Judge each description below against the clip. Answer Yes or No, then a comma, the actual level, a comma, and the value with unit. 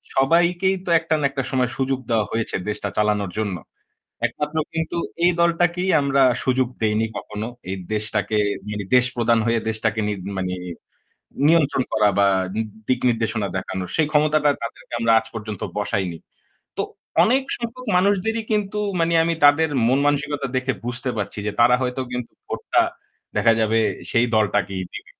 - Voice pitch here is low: Yes, low, 125 Hz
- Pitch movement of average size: No, wide, 6.5 semitones